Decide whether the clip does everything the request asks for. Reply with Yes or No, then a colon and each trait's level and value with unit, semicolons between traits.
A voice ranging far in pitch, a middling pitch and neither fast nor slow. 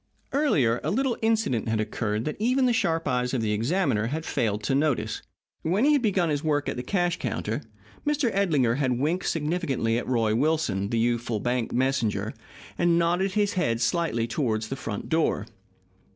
Yes: wide, 7.4 semitones; medium, 145 Hz; average, 180 wpm